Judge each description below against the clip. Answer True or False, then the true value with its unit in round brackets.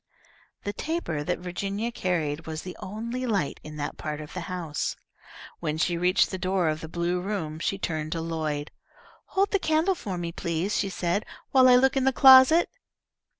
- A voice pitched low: False (180 Hz)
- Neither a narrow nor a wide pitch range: False (6.5 semitones)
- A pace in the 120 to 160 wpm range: False (190 wpm)